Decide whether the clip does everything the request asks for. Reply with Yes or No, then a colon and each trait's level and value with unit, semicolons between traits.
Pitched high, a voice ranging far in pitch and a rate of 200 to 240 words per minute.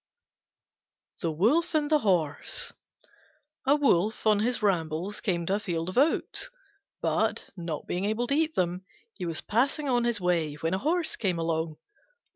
No: high, 195 Hz; wide, 6.8 semitones; average, 165 wpm